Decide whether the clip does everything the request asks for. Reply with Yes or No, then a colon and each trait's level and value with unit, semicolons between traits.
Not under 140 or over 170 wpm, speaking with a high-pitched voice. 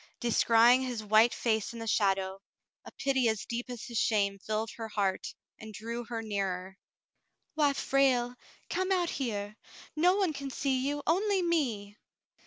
Yes: average, 160 wpm; high, 235 Hz